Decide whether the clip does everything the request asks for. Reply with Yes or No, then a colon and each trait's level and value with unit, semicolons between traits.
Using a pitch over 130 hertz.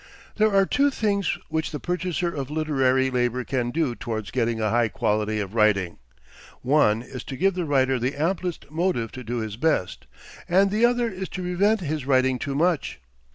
Yes: medium, 140 Hz